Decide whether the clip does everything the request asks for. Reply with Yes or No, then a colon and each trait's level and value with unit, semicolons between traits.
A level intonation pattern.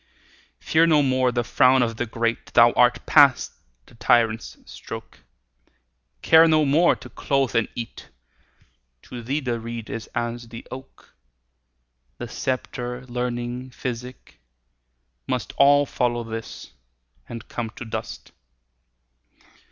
Yes: narrow, 2.0 semitones